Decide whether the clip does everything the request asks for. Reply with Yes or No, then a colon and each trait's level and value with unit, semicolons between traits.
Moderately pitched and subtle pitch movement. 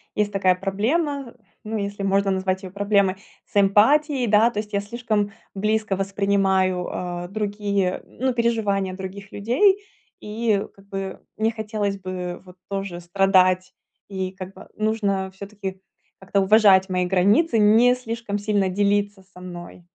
No: high, 200 Hz; narrow, 2.1 semitones